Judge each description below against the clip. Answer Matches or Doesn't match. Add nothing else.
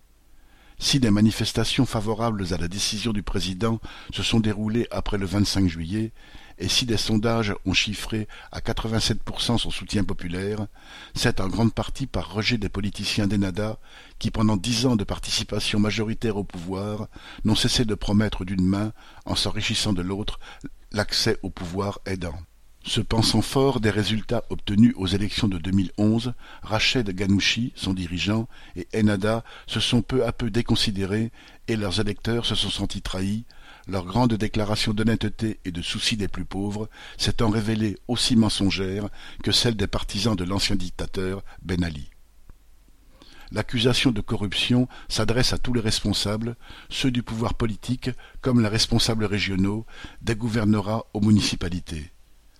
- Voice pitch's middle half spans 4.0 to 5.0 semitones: Doesn't match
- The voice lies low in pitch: Matches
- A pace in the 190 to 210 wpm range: Doesn't match